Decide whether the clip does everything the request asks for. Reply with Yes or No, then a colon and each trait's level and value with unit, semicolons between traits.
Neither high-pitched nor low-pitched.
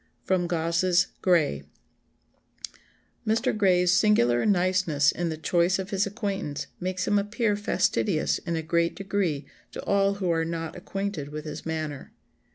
Yes: medium, 180 Hz